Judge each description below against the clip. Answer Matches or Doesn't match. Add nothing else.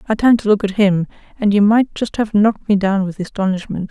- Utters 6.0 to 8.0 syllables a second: Matches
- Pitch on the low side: Doesn't match